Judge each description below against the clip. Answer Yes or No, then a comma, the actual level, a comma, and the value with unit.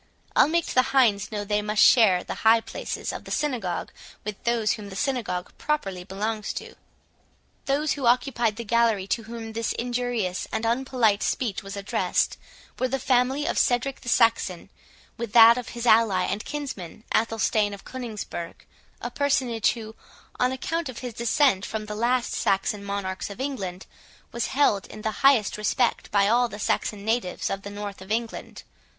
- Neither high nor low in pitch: No, high, 225 Hz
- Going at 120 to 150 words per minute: No, average, 175 wpm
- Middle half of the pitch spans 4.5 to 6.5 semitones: No, average, 3.5 semitones